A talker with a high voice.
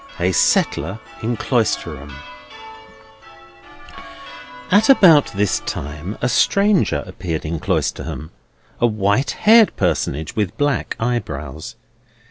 No: low, 105 Hz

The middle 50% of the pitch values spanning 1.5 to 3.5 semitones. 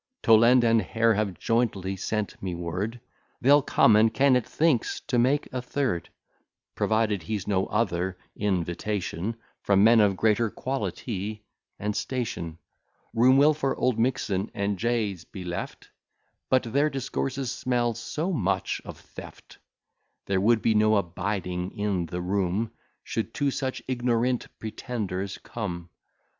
No: average, 4.2 semitones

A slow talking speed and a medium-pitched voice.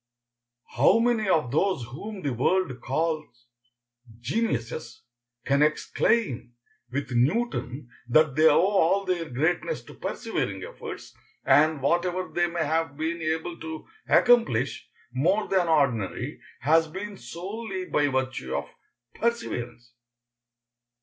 Yes: slow, 115 wpm; medium, 160 Hz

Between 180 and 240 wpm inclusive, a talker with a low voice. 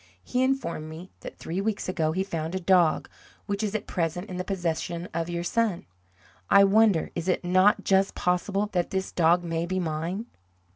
No: average, 190 wpm; medium, 180 Hz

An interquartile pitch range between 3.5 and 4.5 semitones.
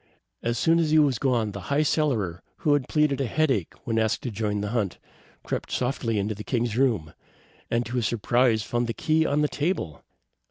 No: average, 4.9 semitones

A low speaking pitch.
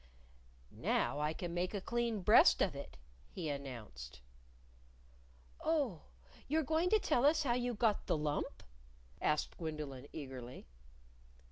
No: medium, 170 Hz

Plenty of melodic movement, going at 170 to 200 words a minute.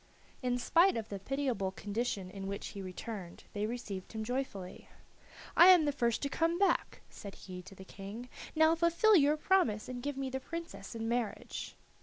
Yes: wide, 6.6 semitones; average, 185 wpm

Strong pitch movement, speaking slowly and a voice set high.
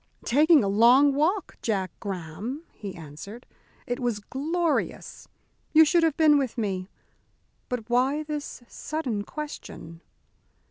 Yes: wide, 6.8 semitones; slow, 125 wpm; very high, 250 Hz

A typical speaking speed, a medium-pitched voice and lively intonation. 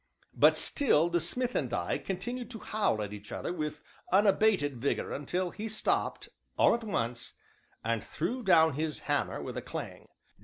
Yes: average, 165 wpm; medium, 170 Hz; wide, 7.5 semitones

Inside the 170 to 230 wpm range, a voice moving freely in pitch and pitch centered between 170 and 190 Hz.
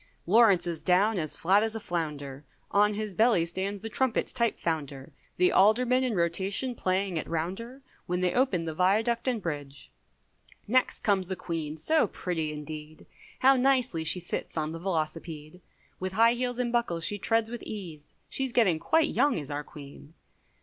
Yes: average, 175 wpm; wide, 6.1 semitones; medium, 185 Hz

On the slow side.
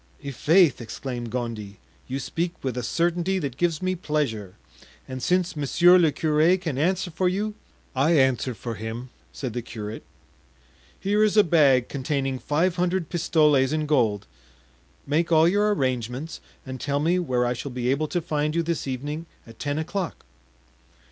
No: average, 165 wpm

